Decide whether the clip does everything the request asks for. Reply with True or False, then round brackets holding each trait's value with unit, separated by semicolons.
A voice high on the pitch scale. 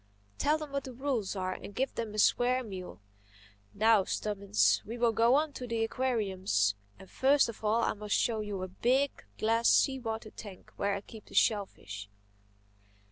True (215 Hz)